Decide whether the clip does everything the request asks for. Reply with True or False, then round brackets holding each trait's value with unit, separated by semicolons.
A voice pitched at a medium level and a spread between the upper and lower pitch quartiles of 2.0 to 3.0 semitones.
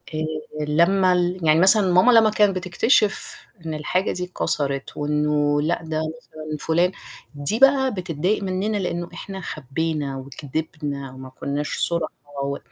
False (160 Hz; 4.0 semitones)